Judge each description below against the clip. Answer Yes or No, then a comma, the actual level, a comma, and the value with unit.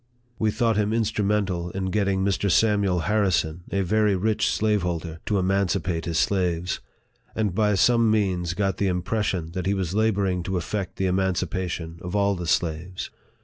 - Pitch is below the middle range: Yes, very low, 95 Hz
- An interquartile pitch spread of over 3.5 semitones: No, average, 2.8 semitones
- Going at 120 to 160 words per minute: No, average, 175 wpm